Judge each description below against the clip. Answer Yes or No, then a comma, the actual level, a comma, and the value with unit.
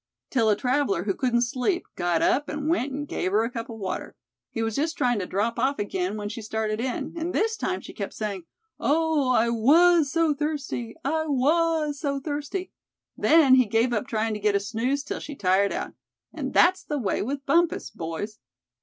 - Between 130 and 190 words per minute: No, fast, 205 wpm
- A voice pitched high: Yes, very high, 255 Hz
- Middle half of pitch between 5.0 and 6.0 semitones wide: Yes, wide, 5.6 semitones